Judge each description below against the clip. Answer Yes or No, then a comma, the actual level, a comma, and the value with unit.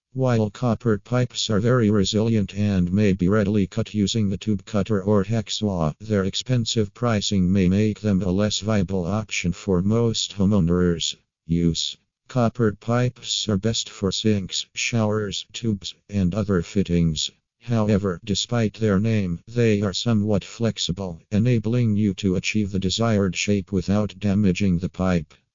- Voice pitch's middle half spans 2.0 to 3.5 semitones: Yes, average, 2.8 semitones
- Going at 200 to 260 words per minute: No, average, 145 wpm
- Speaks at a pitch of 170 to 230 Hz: No, low, 105 Hz